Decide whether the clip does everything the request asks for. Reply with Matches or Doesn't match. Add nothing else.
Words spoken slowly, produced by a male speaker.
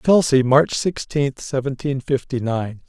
Matches